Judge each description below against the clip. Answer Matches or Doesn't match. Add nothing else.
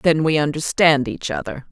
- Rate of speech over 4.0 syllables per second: Matches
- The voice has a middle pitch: Matches